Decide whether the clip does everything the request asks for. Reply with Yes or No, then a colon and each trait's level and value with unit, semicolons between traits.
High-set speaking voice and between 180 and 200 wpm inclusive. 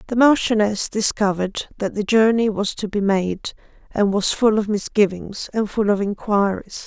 No: high, 205 Hz; average, 165 wpm